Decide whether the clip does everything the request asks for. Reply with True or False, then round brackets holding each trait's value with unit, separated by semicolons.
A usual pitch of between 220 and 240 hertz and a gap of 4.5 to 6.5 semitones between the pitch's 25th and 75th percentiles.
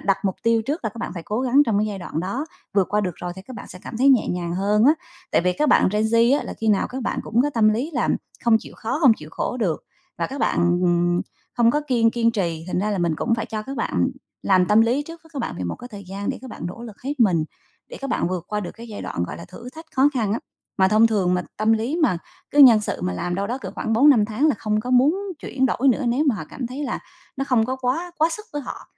True (225 Hz; 5.1 semitones)